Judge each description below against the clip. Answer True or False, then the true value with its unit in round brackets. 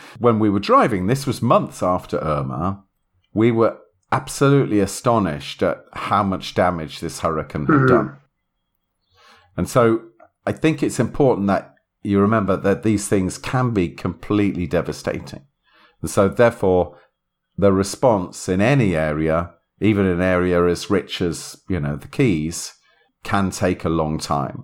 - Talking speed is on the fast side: False (145 wpm)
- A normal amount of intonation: True (3.4 semitones)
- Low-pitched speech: True (95 Hz)